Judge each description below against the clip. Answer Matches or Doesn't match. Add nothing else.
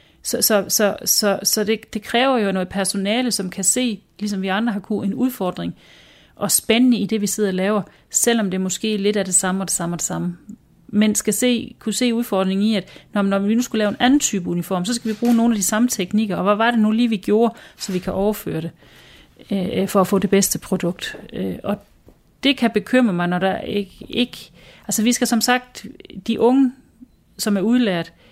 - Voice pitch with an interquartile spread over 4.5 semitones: Doesn't match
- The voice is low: Doesn't match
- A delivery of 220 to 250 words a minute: Matches